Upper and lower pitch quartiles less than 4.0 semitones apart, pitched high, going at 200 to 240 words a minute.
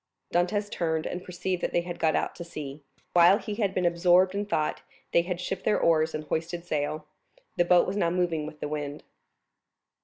No: narrow, 2.5 semitones; medium, 175 Hz; fast, 205 wpm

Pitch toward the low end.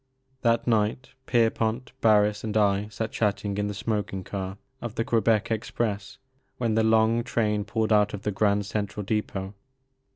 Yes: low, 105 Hz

